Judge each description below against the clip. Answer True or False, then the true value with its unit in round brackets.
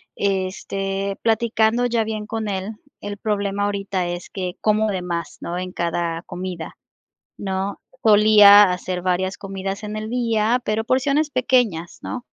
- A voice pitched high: True (200 Hz)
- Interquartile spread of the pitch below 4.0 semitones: True (2.8 semitones)